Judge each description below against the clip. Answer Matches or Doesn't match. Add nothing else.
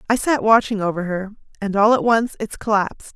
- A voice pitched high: Matches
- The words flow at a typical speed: Doesn't match